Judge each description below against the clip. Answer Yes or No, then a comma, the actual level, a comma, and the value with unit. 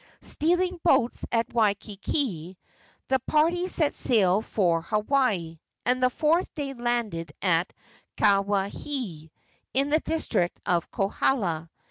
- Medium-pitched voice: No, high, 225 Hz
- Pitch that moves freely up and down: Yes, wide, 7.5 semitones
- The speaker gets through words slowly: Yes, slow, 110 wpm